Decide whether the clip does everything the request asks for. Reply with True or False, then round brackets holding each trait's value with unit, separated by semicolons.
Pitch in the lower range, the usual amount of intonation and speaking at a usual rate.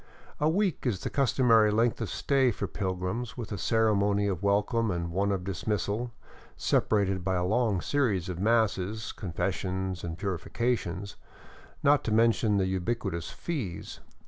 True (100 Hz; 3.8 semitones; 150 wpm)